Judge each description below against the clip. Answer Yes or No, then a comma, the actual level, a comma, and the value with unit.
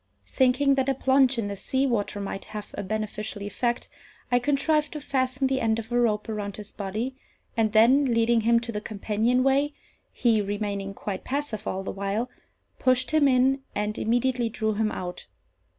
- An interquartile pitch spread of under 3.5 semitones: No, average, 3.9 semitones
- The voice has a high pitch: Yes, high, 230 Hz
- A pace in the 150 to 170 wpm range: No, average, 180 wpm